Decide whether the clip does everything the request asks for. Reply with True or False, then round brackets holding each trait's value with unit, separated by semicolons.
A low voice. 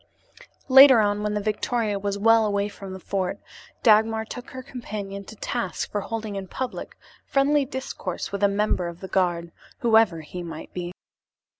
False (210 Hz)